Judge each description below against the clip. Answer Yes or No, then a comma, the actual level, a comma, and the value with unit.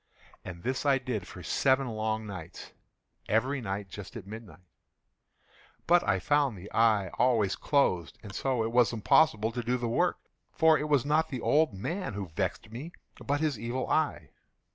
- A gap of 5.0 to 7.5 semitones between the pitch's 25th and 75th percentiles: Yes, wide, 5.4 semitones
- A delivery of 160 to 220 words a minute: Yes, average, 165 wpm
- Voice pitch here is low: Yes, low, 115 Hz